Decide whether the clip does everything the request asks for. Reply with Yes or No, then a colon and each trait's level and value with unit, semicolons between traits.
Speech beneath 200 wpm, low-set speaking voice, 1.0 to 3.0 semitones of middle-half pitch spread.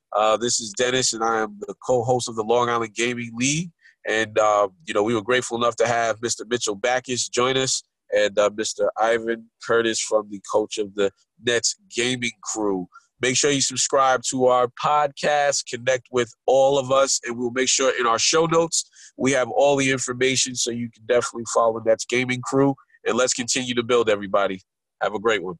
No: fast, 205 wpm; low, 120 Hz; narrow, 2.4 semitones